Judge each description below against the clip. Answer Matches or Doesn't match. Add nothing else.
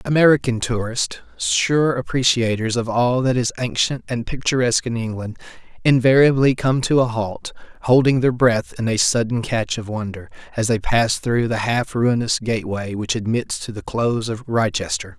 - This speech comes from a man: Matches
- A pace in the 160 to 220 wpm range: Matches